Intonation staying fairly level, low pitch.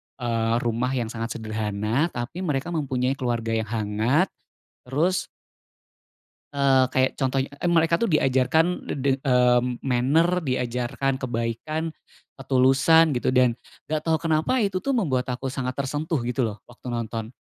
No: average, 4.3 semitones; low, 130 Hz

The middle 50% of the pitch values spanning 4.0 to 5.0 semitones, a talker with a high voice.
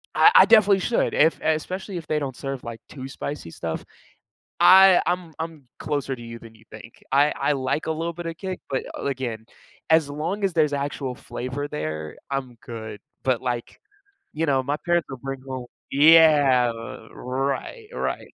No: average, 4.4 semitones; medium, 140 Hz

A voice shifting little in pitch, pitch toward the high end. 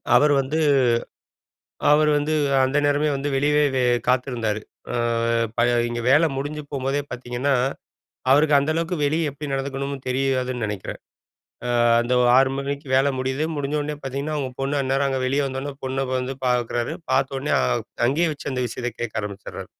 No: narrow, 2.1 semitones; low, 135 Hz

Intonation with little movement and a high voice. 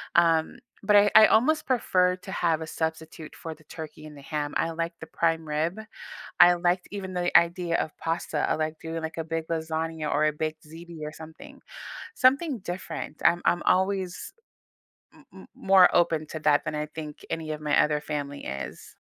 No: narrow, 2.3 semitones; medium, 165 Hz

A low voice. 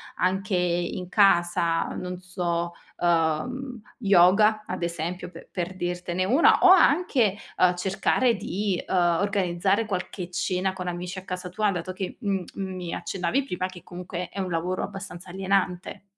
No: medium, 185 Hz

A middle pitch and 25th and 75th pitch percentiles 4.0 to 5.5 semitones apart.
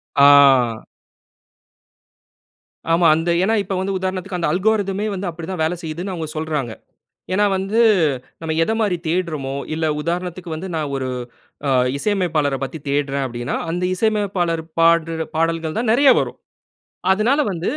No: medium, 170 Hz; average, 3.4 semitones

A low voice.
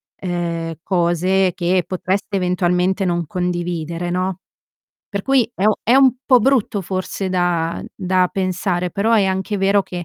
No: medium, 185 Hz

